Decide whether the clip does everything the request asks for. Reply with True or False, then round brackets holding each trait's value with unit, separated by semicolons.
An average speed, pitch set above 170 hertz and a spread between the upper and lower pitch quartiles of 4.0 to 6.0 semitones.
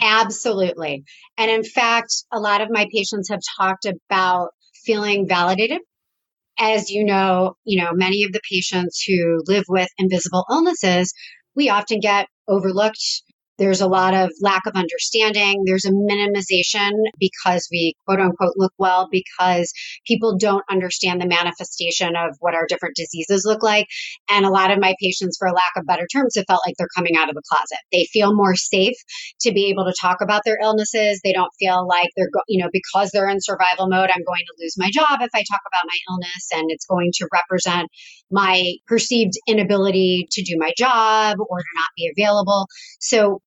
False (185 wpm; 190 Hz; 2.5 semitones)